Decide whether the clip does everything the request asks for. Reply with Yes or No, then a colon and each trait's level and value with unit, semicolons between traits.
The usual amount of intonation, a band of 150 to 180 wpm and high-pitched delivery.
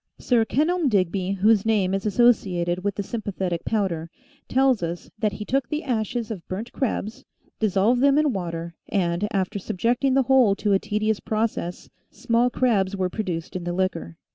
Yes: average, 4.3 semitones; average, 170 wpm; high, 210 Hz